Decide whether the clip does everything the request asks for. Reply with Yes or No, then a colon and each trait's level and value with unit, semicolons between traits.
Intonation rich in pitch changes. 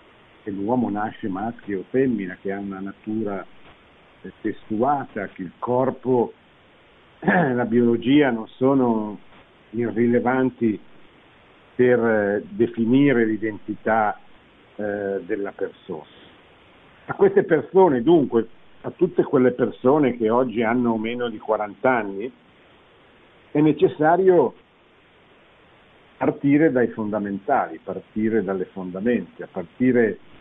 No: average, 3.6 semitones